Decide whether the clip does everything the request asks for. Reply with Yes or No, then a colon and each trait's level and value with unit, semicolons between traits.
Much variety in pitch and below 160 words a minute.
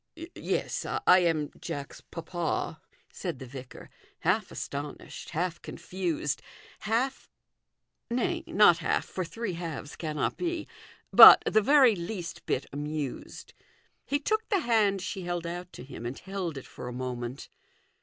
Yes: wide, 6.3 semitones; average, 145 wpm